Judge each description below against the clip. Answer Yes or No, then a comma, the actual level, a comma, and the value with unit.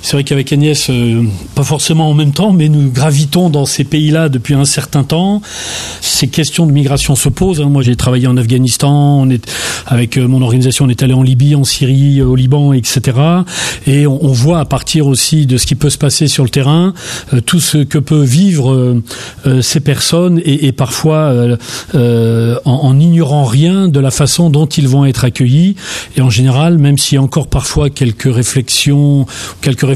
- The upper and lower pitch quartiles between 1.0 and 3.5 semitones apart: Yes, average, 2.8 semitones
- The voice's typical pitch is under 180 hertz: Yes, medium, 140 Hz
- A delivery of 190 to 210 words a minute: Yes, average, 205 wpm